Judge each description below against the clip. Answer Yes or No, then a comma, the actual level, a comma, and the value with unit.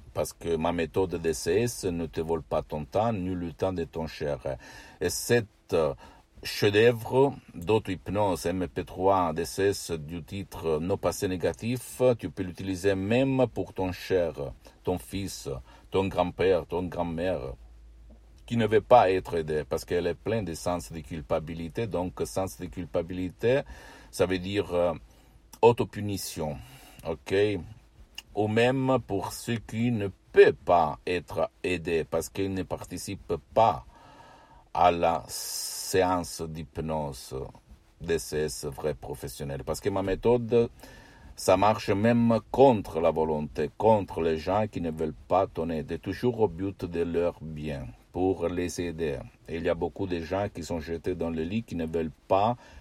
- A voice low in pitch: Yes, very low, 90 Hz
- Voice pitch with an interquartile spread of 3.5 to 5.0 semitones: Yes, average, 4.1 semitones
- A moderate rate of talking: Yes, average, 150 wpm